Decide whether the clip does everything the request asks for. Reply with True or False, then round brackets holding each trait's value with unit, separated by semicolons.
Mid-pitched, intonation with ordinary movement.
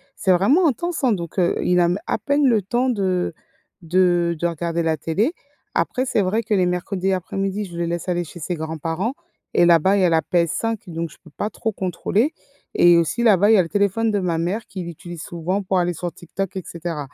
True (180 Hz; 3.2 semitones)